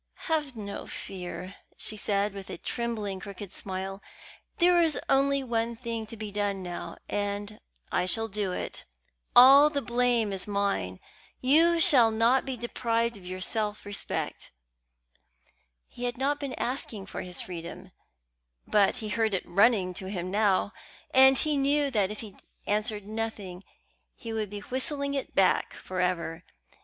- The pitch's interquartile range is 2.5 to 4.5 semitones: Yes, average, 4.1 semitones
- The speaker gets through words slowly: No, average, 155 wpm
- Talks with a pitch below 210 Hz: No, high, 215 Hz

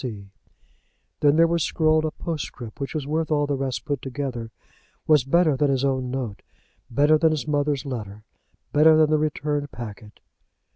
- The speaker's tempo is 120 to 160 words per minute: No, average, 175 wpm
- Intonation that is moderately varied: Yes, average, 3.3 semitones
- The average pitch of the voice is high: No, medium, 145 Hz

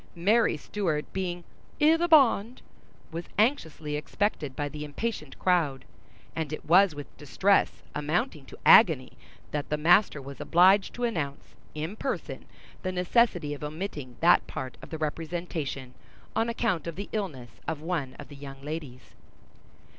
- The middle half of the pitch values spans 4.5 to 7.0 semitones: Yes, average, 5.2 semitones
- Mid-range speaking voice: Yes, medium, 165 Hz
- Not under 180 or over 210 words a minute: No, average, 150 wpm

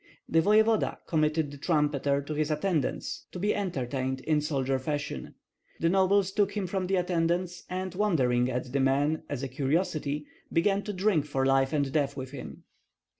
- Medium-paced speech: Yes, average, 175 wpm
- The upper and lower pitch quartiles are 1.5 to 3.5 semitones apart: No, average, 5.1 semitones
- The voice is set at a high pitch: No, medium, 155 Hz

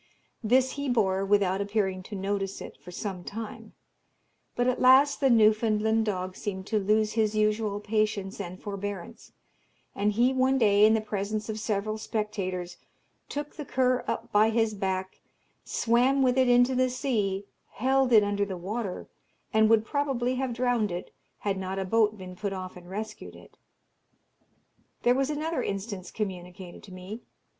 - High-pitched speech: Yes, high, 215 Hz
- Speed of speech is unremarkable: Yes, average, 165 wpm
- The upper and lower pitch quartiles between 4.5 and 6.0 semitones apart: No, average, 3.7 semitones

